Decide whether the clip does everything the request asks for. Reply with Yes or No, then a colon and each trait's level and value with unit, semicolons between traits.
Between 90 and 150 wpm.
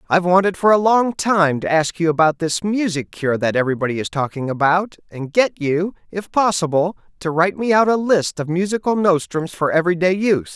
No: fast, 205 wpm